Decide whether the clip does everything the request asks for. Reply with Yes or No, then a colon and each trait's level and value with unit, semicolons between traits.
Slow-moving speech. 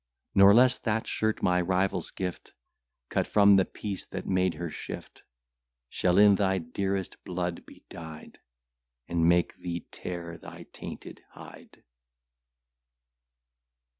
Yes: slow, 125 wpm